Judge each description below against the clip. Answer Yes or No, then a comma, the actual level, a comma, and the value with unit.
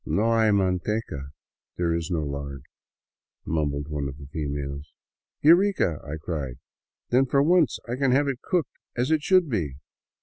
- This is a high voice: No, very low, 90 Hz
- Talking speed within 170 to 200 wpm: Yes, average, 195 wpm